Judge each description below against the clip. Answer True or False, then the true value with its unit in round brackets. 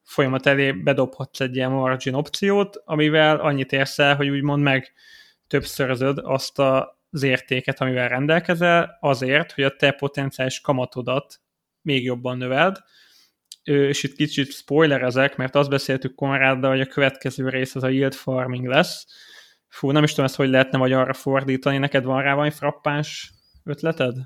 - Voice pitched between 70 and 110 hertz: False (135 Hz)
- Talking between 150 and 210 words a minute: True (155 wpm)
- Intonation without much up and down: True (1.8 semitones)